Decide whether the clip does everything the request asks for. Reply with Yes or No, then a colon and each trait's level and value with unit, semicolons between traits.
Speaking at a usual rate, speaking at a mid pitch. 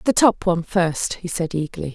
No: fast, 215 wpm; medium, 175 Hz